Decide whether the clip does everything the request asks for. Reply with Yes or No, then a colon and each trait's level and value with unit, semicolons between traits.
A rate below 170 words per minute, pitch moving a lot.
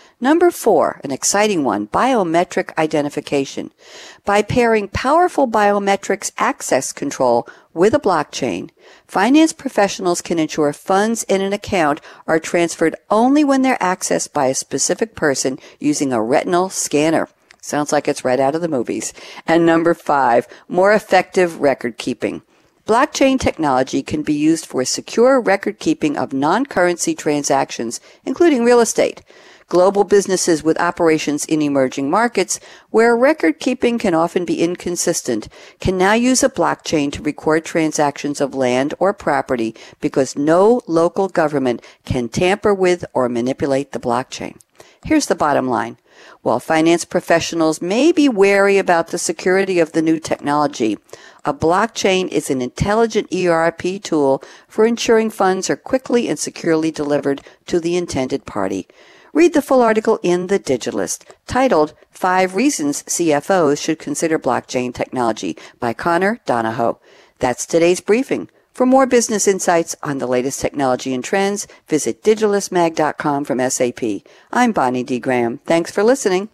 Yes: average, 145 wpm; wide, 5.9 semitones